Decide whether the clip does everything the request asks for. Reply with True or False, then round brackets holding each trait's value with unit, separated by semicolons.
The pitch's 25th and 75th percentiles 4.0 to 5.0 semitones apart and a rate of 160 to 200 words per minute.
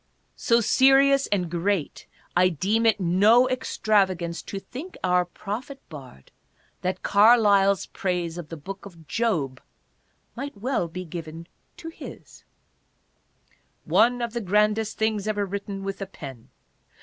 False (4.4 semitones; 135 wpm)